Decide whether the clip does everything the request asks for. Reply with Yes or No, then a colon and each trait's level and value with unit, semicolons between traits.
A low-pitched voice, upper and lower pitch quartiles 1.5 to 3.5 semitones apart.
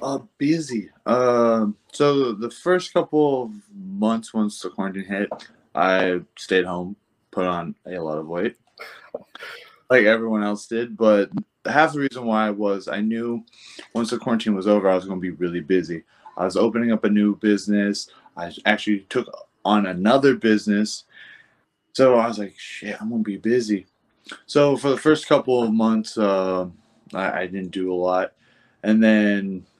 Yes: low, 110 Hz; average, 3.2 semitones